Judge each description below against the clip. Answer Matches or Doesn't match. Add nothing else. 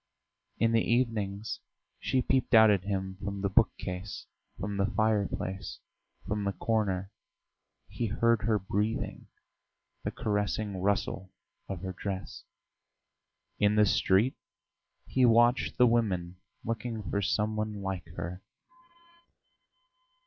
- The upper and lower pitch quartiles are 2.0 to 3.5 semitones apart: Matches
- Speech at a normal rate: Doesn't match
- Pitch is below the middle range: Matches